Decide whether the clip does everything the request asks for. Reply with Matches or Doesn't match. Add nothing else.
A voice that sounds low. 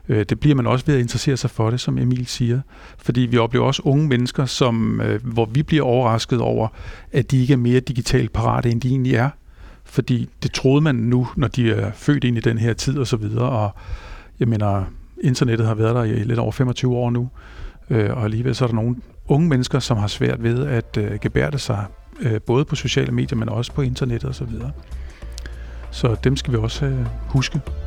Matches